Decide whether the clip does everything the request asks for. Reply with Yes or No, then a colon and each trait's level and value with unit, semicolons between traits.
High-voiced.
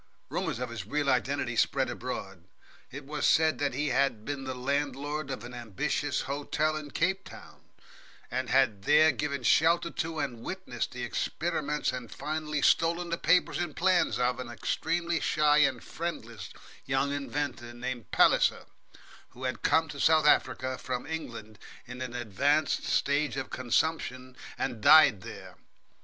No: medium, 140 Hz